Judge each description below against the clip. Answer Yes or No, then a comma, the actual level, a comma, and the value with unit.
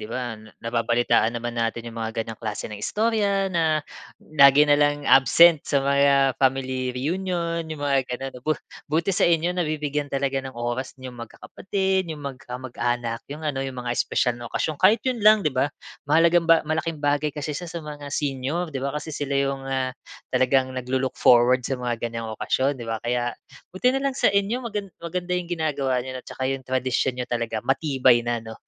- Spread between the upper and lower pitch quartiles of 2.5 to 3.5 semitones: No, average, 4.4 semitones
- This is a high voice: No, medium, 140 Hz